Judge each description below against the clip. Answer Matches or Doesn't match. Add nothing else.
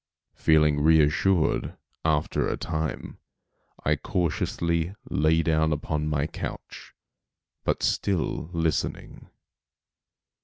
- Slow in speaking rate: Matches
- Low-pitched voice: Matches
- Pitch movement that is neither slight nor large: Doesn't match